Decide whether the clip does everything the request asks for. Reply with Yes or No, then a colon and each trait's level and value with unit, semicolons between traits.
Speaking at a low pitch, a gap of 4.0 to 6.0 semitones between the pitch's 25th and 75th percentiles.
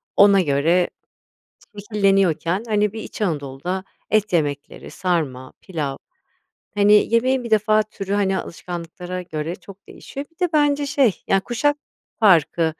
No: high, 195 Hz; average, 4.3 semitones